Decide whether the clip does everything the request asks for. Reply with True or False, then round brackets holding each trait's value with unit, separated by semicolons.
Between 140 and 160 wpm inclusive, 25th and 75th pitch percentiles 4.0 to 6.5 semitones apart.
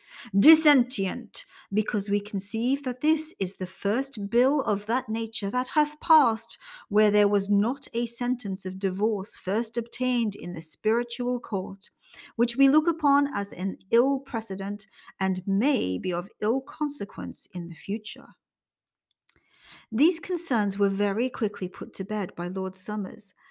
True (150 wpm; 4.3 semitones)